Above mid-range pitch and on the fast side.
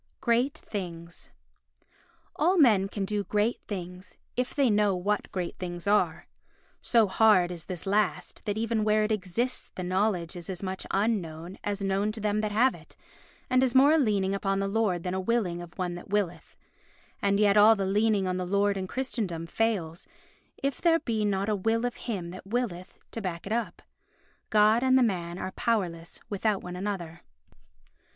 No: high, 200 Hz; average, 185 wpm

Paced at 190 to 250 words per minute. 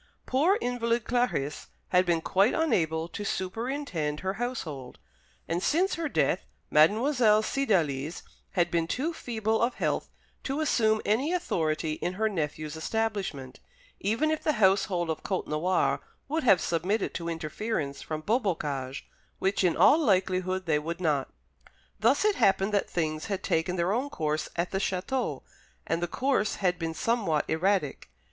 No: average, 150 wpm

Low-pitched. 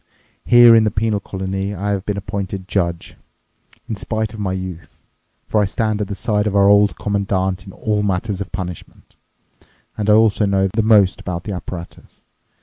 Yes: low, 100 Hz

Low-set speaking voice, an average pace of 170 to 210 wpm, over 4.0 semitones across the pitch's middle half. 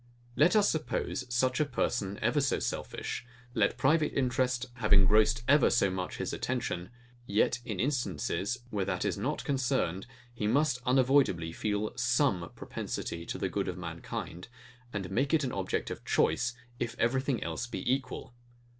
No: low, 120 Hz; average, 160 wpm; average, 5.0 semitones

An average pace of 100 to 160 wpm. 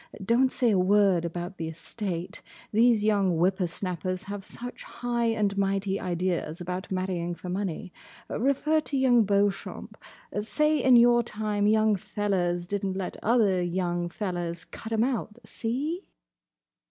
Yes: average, 145 wpm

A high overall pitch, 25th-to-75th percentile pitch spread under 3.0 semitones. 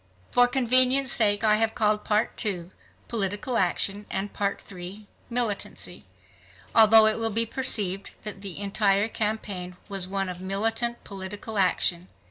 Yes: high, 210 Hz; narrow, 2.5 semitones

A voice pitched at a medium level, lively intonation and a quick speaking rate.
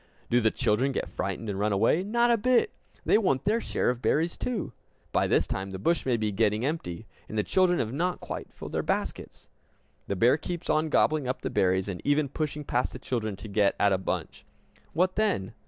No: low, 130 Hz; wide, 8.4 semitones; fast, 220 wpm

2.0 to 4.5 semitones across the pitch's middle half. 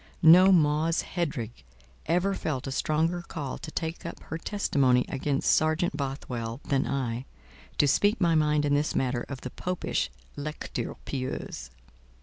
Yes: average, 3.9 semitones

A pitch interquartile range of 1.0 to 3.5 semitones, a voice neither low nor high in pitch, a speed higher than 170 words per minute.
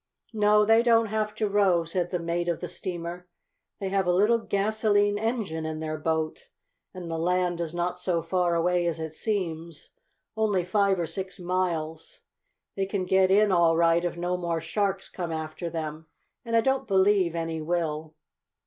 Yes: average, 3.2 semitones; medium, 180 Hz; average, 180 wpm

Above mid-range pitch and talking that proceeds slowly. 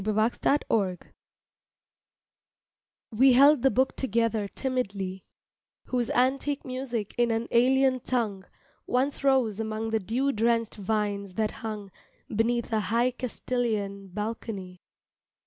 Yes: high, 230 Hz; slow, 120 wpm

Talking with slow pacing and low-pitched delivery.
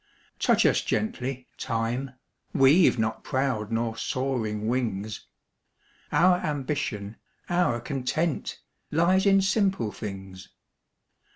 Yes: slow, 95 wpm; low, 130 Hz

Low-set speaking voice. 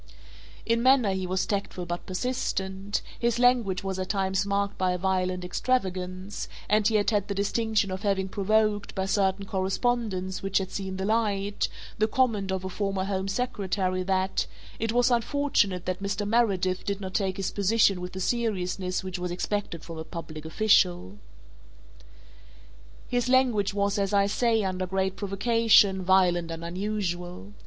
No: high, 195 Hz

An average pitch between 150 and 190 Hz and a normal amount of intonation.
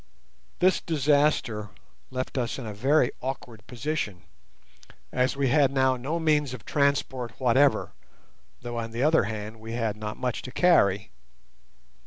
No: low, 130 Hz; average, 4.0 semitones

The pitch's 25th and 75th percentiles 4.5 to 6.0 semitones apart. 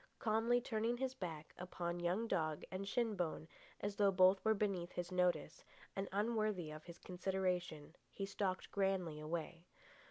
No: average, 3.3 semitones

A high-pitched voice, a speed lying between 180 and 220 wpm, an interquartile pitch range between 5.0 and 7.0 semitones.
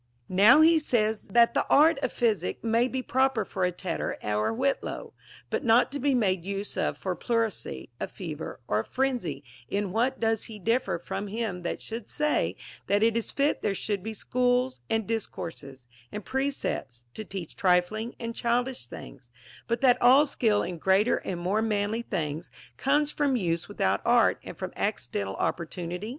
Yes: high, 220 Hz; average, 185 wpm; wide, 5.4 semitones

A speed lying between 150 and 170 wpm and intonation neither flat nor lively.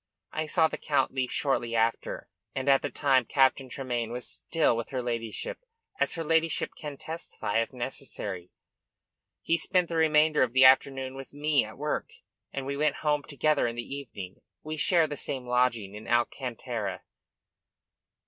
Yes: average, 165 wpm; average, 4.1 semitones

